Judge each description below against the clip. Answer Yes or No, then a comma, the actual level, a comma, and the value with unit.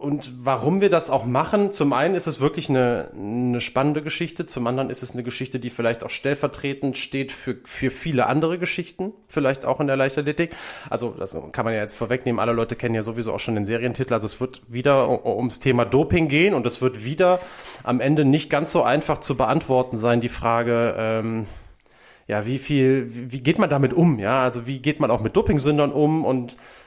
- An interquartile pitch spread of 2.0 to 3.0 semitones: No, average, 3.8 semitones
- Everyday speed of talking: No, fast, 210 wpm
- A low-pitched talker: Yes, low, 130 Hz